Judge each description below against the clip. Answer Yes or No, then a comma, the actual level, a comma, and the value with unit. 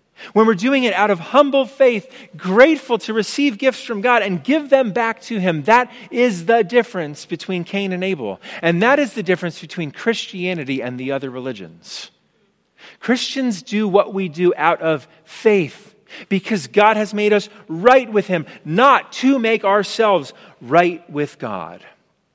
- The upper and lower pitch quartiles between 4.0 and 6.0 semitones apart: Yes, wide, 5.4 semitones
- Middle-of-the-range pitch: No, high, 210 Hz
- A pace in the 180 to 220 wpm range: No, average, 165 wpm